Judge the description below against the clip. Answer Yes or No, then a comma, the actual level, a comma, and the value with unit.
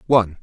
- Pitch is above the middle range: No, low, 105 Hz